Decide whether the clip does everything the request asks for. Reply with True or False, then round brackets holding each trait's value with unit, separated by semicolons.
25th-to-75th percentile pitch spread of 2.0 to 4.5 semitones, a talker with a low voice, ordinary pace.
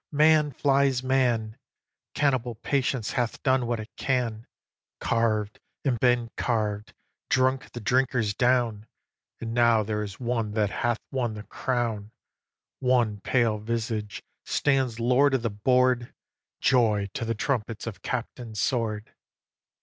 False (2.9 semitones; 120 Hz; 130 wpm)